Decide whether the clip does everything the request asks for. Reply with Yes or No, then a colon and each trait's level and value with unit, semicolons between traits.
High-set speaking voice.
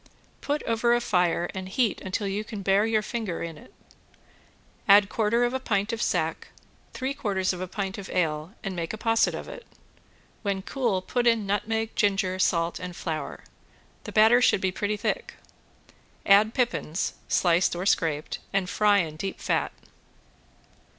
Yes: high, 200 Hz